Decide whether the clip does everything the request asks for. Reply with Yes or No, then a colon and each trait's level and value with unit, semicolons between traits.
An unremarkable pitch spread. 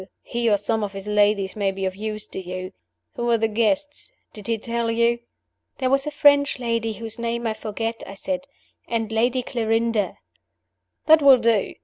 No: narrow, 2.3 semitones